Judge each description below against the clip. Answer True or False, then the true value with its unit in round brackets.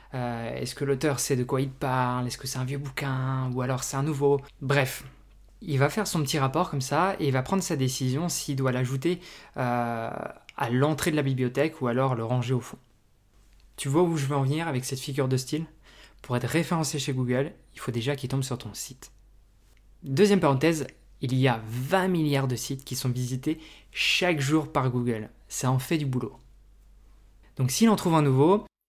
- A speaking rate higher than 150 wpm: True (210 wpm)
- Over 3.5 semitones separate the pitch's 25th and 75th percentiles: False (3.0 semitones)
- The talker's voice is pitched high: False (135 Hz)